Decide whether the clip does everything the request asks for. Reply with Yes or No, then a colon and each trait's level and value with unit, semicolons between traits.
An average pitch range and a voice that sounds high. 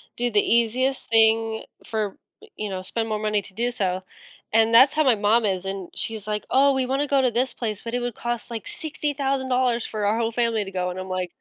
Yes: average, 3.2 semitones; high, 225 Hz